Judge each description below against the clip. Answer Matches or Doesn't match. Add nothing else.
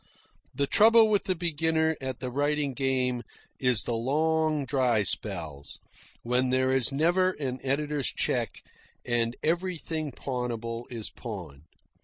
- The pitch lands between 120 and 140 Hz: Matches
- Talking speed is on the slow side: Matches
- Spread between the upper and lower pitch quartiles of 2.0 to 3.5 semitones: Doesn't match